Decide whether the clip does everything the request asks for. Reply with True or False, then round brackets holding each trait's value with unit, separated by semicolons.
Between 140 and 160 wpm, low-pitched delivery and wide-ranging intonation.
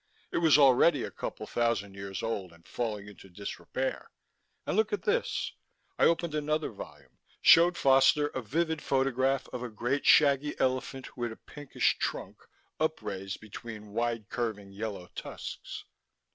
True (150 wpm; 125 Hz; 5.8 semitones)